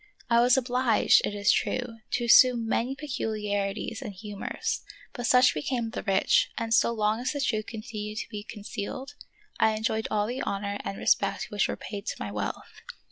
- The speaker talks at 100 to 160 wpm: No, average, 190 wpm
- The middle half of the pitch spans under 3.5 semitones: Yes, average, 2.8 semitones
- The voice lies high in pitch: Yes, high, 220 Hz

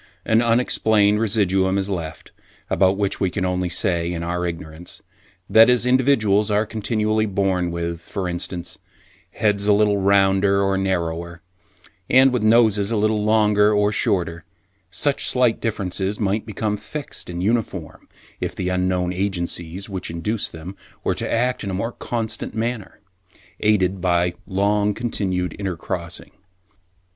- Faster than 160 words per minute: No, average, 145 wpm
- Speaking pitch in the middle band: No, low, 100 Hz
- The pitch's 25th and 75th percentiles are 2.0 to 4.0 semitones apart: Yes, average, 3.0 semitones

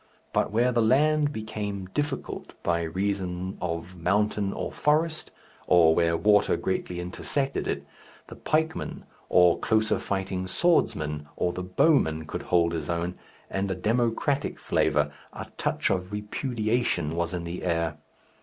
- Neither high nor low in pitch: No, very low, 95 Hz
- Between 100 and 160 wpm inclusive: Yes, average, 140 wpm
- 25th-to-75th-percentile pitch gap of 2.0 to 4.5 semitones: No, average, 5.1 semitones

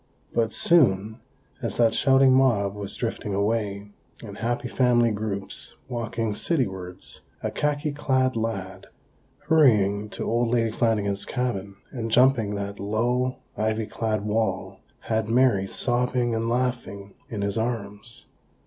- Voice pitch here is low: Yes, low, 115 Hz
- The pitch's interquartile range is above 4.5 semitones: No, average, 3.4 semitones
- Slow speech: Yes, slow, 130 wpm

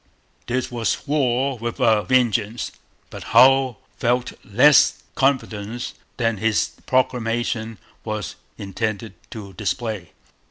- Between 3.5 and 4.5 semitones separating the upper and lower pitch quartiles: No, average, 2.9 semitones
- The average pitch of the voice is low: Yes, low, 115 Hz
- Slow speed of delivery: Yes, slow, 105 wpm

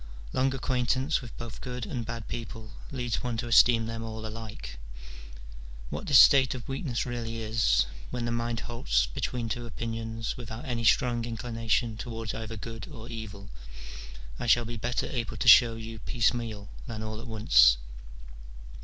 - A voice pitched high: No, low, 115 Hz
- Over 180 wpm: No, average, 160 wpm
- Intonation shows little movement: Yes, narrow, 1.5 semitones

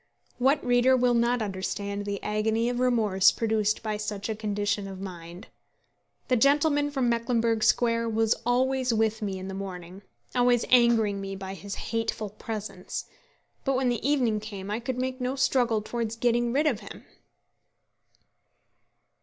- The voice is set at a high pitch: Yes, high, 225 Hz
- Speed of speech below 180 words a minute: Yes, average, 155 wpm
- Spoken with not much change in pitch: No, average, 3.3 semitones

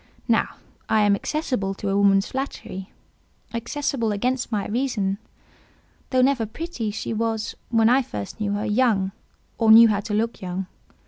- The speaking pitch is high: Yes, high, 220 Hz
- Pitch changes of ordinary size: Yes, average, 3.4 semitones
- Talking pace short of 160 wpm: Yes, average, 140 wpm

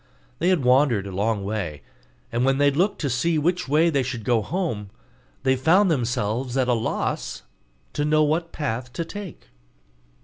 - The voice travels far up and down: Yes, wide, 5.7 semitones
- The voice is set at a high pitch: No, low, 135 Hz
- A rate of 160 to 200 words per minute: Yes, average, 175 wpm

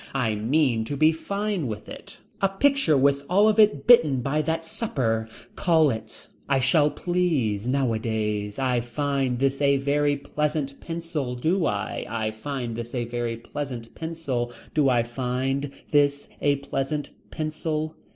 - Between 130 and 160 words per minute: Yes, average, 150 wpm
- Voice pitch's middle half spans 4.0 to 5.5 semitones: Yes, average, 4.6 semitones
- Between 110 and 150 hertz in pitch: Yes, medium, 140 Hz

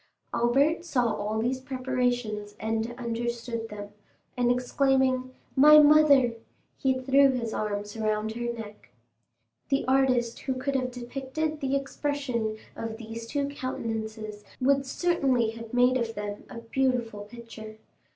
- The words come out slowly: Yes, slow, 130 wpm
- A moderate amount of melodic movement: Yes, average, 3.1 semitones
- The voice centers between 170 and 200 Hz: No, high, 245 Hz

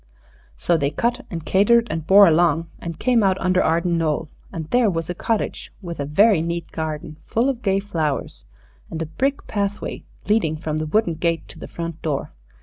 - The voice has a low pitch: No, medium, 170 Hz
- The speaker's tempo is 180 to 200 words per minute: Yes, average, 195 wpm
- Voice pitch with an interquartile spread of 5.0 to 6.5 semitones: No, average, 4.3 semitones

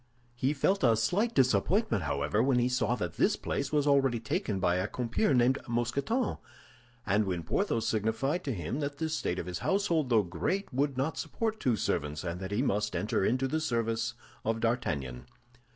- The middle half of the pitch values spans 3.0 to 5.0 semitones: No, wide, 5.5 semitones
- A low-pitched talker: Yes, low, 120 Hz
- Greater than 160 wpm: Yes, average, 185 wpm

